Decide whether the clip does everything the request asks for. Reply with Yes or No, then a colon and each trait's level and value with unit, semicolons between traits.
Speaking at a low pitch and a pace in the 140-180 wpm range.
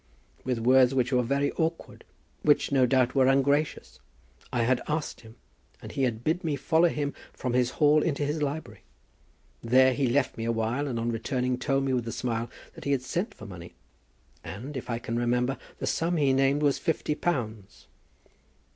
No: low, 130 Hz; average, 190 wpm